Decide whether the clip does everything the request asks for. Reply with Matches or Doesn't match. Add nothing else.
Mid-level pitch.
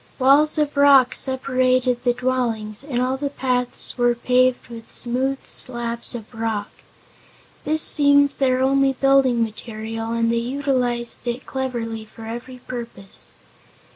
Doesn't match